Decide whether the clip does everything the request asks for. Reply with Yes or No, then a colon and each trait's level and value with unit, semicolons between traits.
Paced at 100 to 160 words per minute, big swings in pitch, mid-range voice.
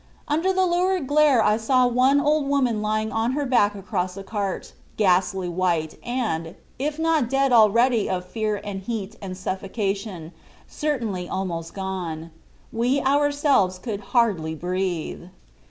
No: average, 140 wpm; wide, 6.3 semitones; high, 215 Hz